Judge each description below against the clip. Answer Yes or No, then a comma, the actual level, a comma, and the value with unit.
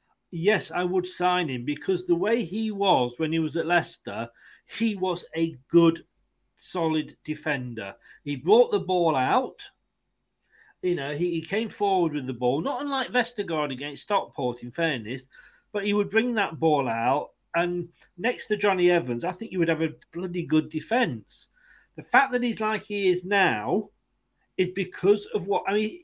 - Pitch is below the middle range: No, medium, 175 Hz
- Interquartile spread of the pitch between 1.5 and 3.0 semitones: No, average, 4.7 semitones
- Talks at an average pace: Yes, average, 175 wpm